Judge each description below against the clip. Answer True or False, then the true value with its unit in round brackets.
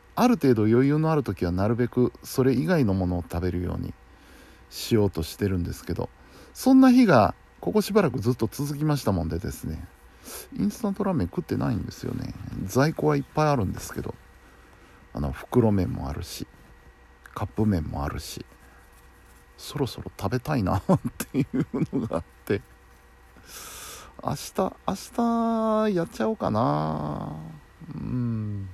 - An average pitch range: False (8.6 semitones)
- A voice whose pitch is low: True (110 Hz)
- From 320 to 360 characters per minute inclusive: False (310 characters per minute)